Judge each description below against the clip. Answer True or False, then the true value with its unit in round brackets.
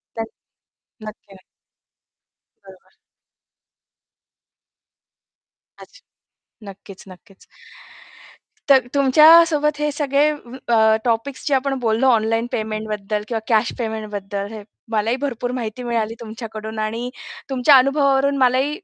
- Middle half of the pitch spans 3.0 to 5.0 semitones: True (3.9 semitones)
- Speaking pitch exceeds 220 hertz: True (230 Hz)